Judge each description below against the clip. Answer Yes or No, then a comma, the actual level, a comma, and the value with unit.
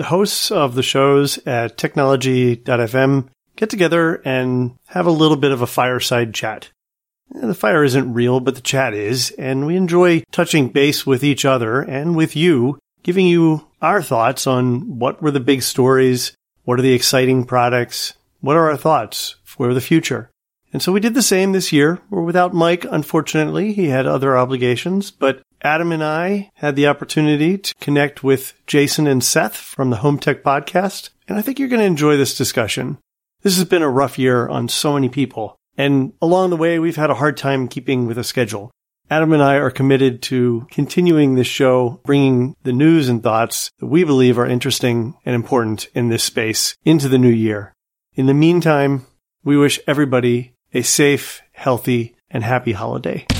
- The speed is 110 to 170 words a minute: No, average, 185 wpm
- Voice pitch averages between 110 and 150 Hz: Yes, low, 135 Hz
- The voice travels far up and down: No, average, 4.0 semitones